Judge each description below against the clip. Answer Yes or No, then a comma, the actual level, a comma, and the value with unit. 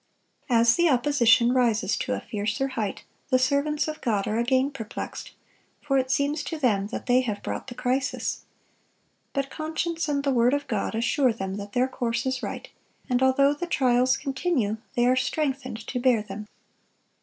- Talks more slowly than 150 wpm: No, average, 180 wpm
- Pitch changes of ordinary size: Yes, average, 3.4 semitones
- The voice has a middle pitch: No, very high, 255 Hz